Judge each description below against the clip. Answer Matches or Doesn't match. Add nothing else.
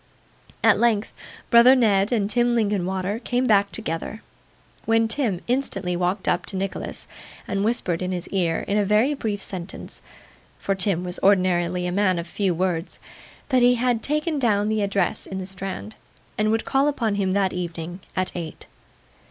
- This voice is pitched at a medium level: Doesn't match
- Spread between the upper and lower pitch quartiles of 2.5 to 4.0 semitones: Matches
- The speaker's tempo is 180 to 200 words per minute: Doesn't match